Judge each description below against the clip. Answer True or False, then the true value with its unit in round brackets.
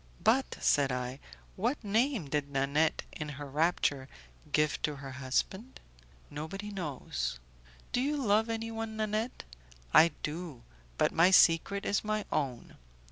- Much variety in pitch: True (7.3 semitones)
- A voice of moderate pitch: True (165 Hz)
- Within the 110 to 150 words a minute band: True (135 wpm)